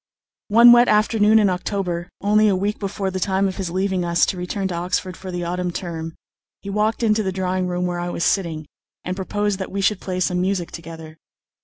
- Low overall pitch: No, medium, 185 Hz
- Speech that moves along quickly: Yes, fast, 215 wpm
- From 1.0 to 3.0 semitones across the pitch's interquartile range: Yes, narrow, 2.4 semitones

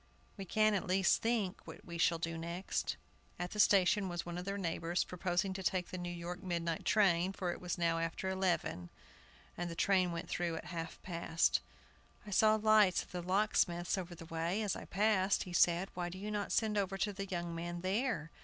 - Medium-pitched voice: Yes, medium, 180 Hz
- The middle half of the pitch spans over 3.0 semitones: No, narrow, 2.5 semitones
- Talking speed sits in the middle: No, fast, 210 wpm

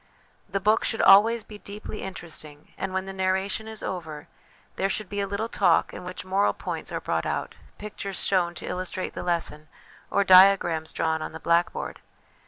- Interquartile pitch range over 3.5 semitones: No, narrow, 2.6 semitones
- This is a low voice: No, high, 190 Hz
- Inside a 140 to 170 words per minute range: No, average, 185 wpm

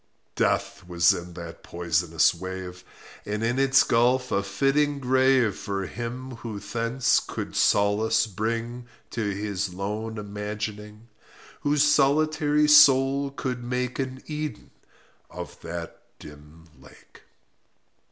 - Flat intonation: No, average, 5.0 semitones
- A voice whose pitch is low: Yes, low, 115 Hz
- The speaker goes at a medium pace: No, slow, 115 wpm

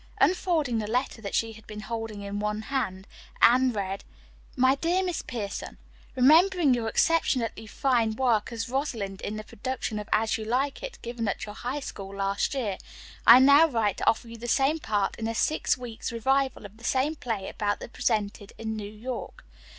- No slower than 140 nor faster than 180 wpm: No, average, 195 wpm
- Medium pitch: No, high, 230 Hz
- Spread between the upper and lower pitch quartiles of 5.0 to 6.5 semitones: No, average, 3.9 semitones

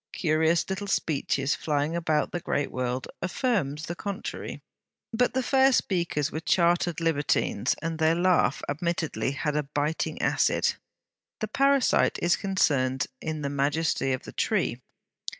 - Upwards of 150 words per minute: No, average, 140 wpm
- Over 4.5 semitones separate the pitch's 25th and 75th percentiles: No, average, 3.9 semitones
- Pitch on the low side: No, medium, 160 Hz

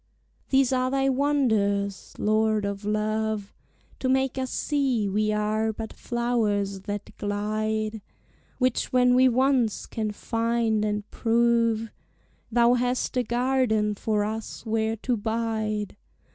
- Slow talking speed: Yes, slow, 125 wpm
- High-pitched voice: Yes, high, 220 Hz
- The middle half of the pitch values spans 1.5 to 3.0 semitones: Yes, average, 2.7 semitones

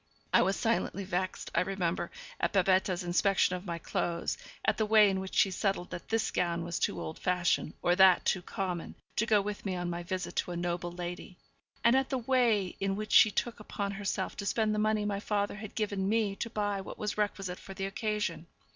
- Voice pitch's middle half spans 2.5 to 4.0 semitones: Yes, average, 2.9 semitones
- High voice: Yes, high, 195 Hz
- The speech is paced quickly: Yes, fast, 220 wpm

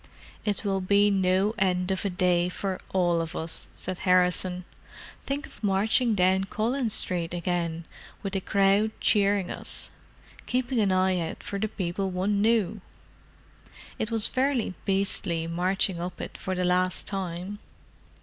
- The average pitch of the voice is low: No, high, 190 Hz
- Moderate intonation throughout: No, narrow, 2.3 semitones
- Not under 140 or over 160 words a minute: Yes, average, 150 wpm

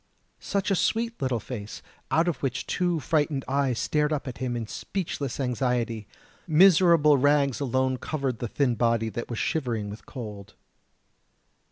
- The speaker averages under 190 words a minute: Yes, average, 155 wpm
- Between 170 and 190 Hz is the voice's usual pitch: No, low, 130 Hz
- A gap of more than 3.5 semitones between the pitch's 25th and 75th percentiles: Yes, average, 4.2 semitones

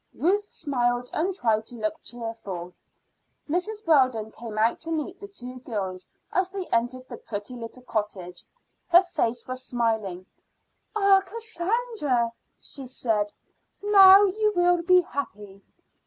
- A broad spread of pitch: Yes, wide, 8.4 semitones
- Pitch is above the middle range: Yes, very high, 255 Hz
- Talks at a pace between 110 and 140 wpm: Yes, slow, 135 wpm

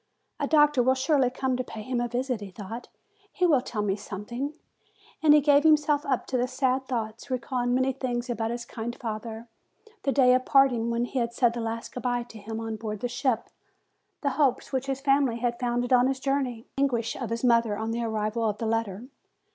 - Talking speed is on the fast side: Yes, fast, 220 wpm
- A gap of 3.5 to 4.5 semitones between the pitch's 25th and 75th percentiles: No, narrow, 2.6 semitones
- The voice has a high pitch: Yes, high, 245 Hz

